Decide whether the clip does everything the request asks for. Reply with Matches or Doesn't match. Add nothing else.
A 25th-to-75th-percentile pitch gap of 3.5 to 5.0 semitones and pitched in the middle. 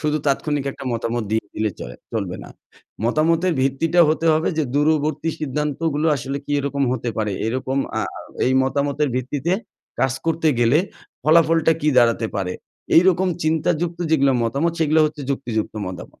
Matches